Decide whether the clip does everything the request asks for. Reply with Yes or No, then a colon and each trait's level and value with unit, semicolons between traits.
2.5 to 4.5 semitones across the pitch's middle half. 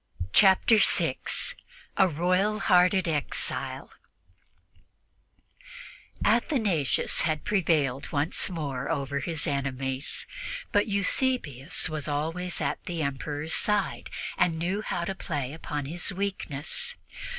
No: average, 4.9 semitones